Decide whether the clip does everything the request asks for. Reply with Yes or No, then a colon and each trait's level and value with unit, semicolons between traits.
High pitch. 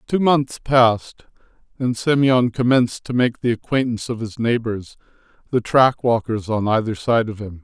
No: low, 120 Hz